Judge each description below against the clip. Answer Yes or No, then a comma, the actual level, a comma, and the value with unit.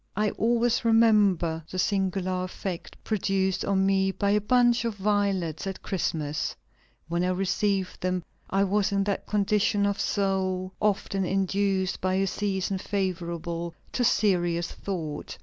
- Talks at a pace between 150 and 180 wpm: No, average, 140 wpm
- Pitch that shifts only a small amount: Yes, narrow, 1.8 semitones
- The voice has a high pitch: Yes, high, 195 Hz